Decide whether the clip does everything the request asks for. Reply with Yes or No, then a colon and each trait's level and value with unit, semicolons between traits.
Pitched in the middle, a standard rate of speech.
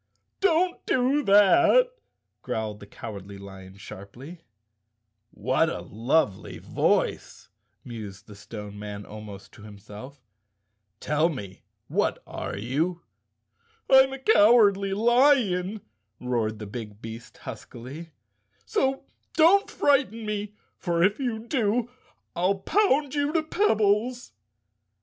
No: medium, 165 Hz; slow, 115 wpm